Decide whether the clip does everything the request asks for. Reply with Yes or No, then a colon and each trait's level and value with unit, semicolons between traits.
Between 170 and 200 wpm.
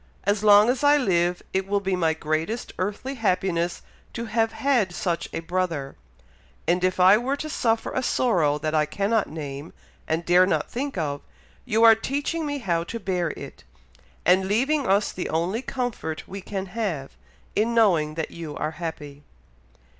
Yes: average, 175 wpm